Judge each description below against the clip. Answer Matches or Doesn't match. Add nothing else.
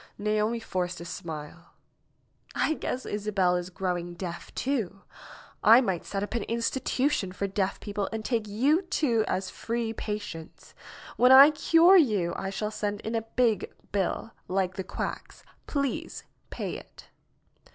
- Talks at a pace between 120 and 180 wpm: Matches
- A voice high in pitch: Matches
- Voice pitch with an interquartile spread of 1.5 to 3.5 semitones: Doesn't match